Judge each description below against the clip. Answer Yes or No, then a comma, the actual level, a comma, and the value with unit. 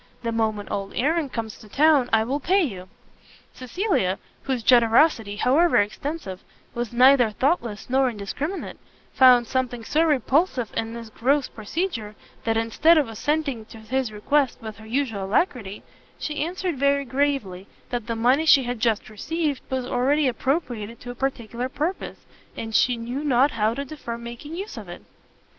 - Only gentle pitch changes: No, average, 4.4 semitones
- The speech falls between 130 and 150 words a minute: No, average, 160 wpm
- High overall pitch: Yes, very high, 250 Hz